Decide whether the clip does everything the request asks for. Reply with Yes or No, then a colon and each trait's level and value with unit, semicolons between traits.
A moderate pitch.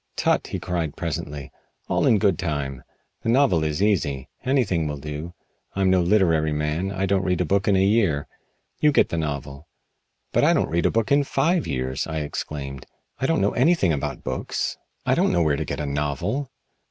No: very low, 85 Hz